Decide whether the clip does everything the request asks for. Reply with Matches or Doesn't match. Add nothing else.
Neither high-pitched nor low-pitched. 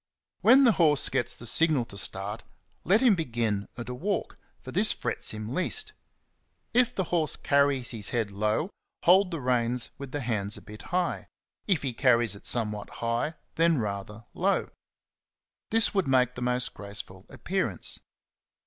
Doesn't match